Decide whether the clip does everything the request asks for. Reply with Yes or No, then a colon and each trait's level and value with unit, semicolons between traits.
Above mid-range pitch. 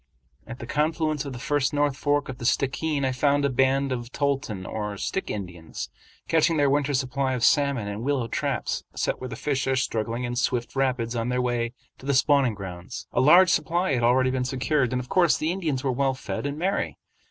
No: low, 130 Hz